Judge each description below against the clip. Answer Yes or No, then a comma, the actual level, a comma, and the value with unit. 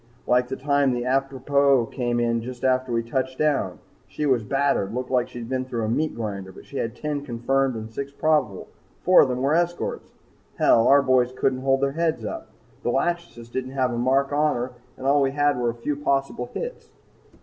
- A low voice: Yes, low, 130 Hz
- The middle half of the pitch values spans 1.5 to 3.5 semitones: Yes, average, 2.7 semitones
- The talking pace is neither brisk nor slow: No, fast, 215 wpm